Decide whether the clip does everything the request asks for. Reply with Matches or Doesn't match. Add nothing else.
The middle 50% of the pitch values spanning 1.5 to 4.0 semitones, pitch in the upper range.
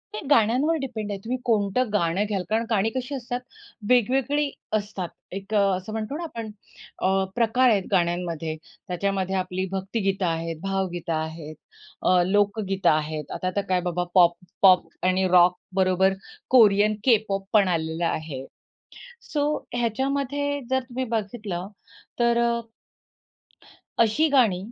Doesn't match